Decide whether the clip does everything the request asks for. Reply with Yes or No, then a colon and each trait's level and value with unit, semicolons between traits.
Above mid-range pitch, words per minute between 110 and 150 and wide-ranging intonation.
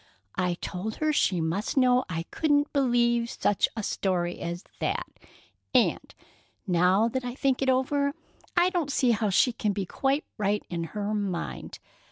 No: high, 220 Hz; average, 165 wpm; wide, 6.1 semitones